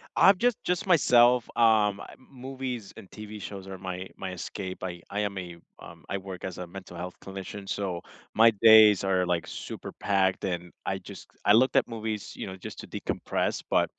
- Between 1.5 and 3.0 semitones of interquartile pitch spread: No, average, 3.5 semitones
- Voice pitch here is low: Yes, low, 100 Hz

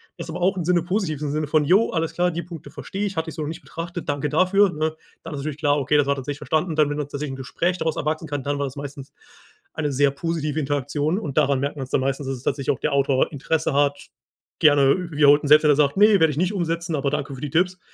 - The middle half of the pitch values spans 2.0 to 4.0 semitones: Yes, average, 2.7 semitones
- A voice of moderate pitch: Yes, medium, 150 Hz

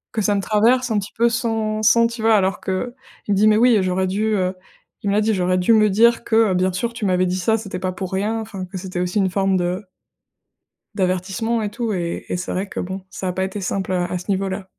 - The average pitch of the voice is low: No, high, 195 Hz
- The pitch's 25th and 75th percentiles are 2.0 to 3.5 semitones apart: Yes, average, 3.0 semitones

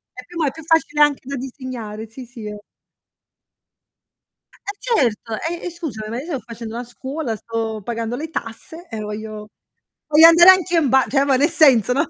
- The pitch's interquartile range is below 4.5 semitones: No, wide, 5.8 semitones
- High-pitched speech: Yes, very high, 255 Hz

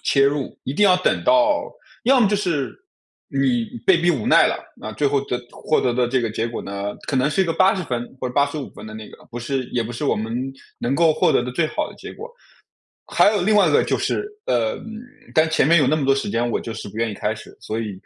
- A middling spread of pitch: No, wide, 6.5 semitones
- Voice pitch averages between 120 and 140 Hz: Yes, low, 135 Hz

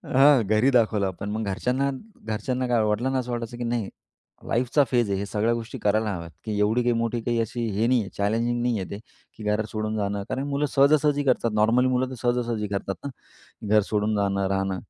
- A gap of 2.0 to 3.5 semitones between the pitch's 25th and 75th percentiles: Yes, average, 2.9 semitones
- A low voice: Yes, low, 115 Hz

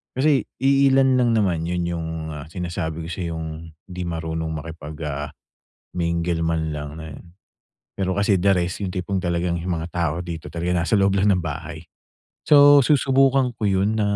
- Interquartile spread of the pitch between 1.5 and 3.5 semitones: No, average, 4.0 semitones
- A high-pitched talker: No, very low, 85 Hz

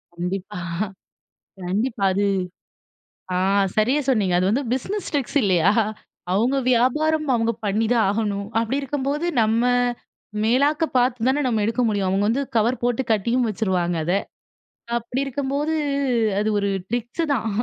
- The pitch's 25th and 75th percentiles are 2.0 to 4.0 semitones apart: No, average, 4.6 semitones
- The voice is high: Yes, high, 230 Hz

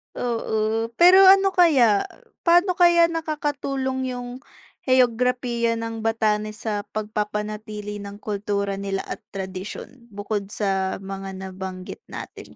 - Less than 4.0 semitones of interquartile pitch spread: No, average, 4.4 semitones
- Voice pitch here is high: Yes, high, 220 Hz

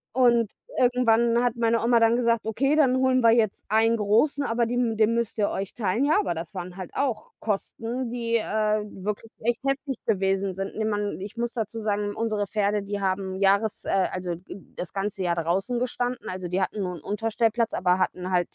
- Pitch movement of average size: Yes, average, 3.3 semitones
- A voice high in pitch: Yes, high, 220 Hz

